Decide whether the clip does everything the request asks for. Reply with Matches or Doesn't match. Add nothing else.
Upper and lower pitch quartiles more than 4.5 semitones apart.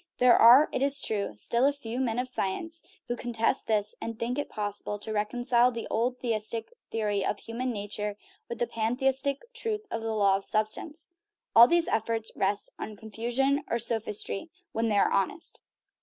Doesn't match